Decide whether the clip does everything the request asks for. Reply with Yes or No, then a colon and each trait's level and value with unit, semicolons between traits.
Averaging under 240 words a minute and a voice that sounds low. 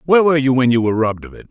No: fast, 360 wpm; low, 130 Hz